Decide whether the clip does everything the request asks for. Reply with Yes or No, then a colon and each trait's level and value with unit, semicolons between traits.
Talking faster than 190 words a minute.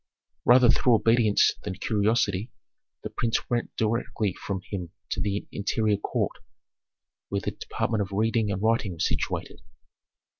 No: average, 140 wpm